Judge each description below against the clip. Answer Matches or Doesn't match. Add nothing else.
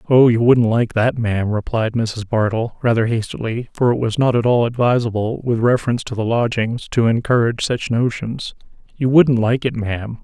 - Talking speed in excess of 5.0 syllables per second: Matches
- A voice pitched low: Matches